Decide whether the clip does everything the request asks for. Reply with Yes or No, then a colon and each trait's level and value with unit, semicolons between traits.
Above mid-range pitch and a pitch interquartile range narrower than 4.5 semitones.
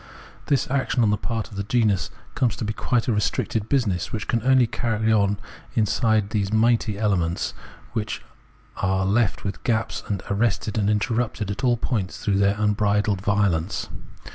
No: low, 105 Hz; narrow, 2.4 semitones